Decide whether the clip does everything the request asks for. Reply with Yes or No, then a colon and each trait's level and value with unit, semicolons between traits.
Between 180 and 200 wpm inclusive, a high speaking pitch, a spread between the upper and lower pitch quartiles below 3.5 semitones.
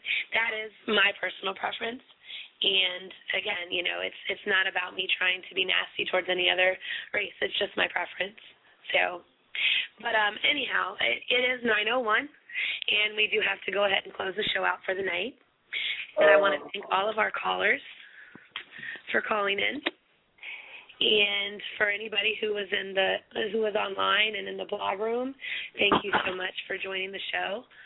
Yes: average, 185 wpm; high, 205 Hz; narrow, 2.4 semitones